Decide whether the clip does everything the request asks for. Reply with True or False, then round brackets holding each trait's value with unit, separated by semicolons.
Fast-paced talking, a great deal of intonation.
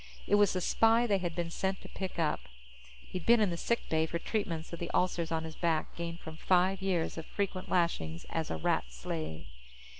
False (215 wpm; 2.9 semitones)